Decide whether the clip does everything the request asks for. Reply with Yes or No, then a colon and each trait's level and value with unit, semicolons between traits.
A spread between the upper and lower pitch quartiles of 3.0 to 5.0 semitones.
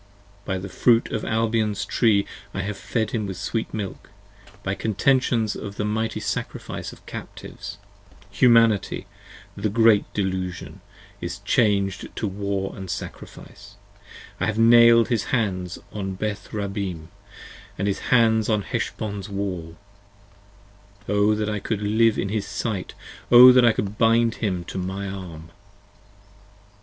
No: narrow, 2.6 semitones